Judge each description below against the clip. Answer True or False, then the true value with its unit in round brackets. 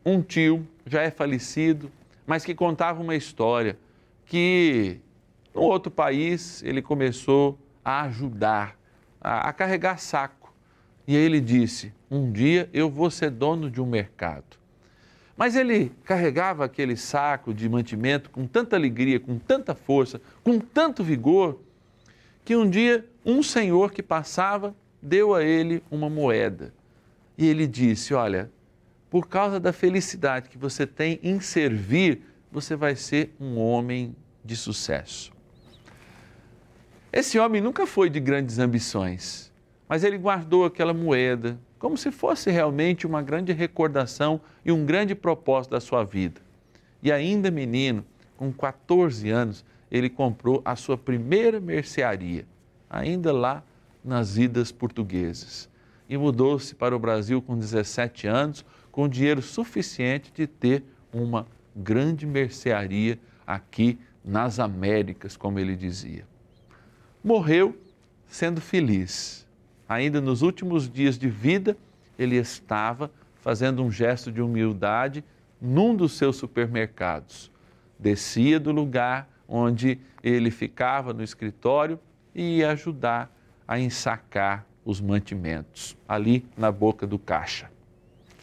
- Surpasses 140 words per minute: False (125 wpm)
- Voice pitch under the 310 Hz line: True (135 Hz)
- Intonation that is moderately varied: False (5.7 semitones)